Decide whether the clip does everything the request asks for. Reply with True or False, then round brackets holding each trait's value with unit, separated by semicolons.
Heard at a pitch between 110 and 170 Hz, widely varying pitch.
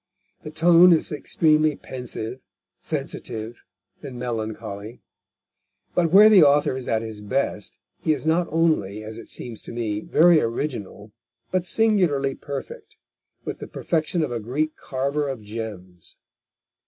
True (135 Hz; 6.0 semitones)